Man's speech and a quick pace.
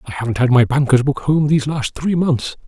Yes: male; fast, 245 wpm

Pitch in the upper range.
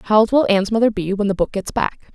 Yes: high, 210 Hz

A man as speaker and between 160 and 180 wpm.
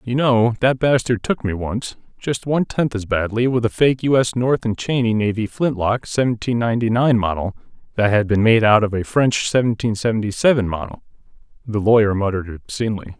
No: male; average, 190 wpm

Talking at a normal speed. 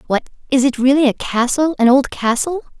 Yes: average, 195 wpm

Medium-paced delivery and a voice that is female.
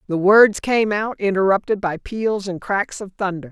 Yes: average, 190 wpm; female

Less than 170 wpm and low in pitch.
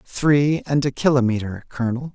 Yes: average, 140 wpm; low, 130 Hz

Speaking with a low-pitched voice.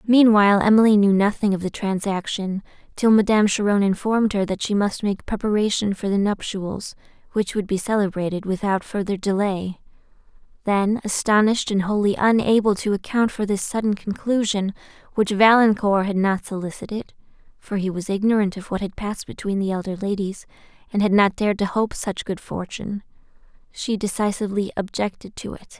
No: high, 205 Hz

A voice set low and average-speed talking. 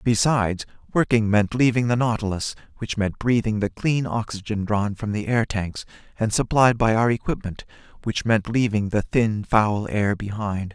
Yes: low, 110 Hz; average, 165 wpm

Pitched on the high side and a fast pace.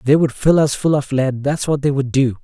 No: medium, 140 Hz; fast, 295 wpm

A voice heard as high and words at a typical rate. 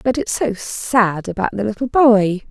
Yes: high, 220 Hz; average, 190 wpm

